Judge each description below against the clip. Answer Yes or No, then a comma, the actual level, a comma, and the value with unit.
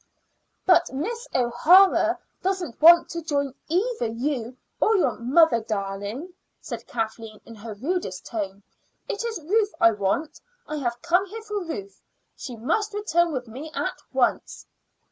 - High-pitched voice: Yes, very high, 300 Hz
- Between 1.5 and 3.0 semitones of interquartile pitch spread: No, wide, 8.2 semitones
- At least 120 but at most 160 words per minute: Yes, average, 145 wpm